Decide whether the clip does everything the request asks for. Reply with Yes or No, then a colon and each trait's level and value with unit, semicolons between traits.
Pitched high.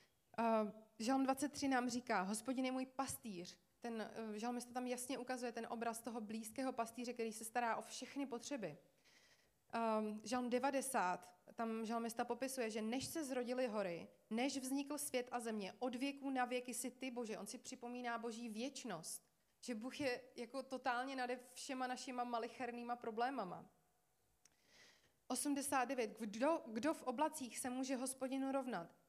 Yes: high, 245 Hz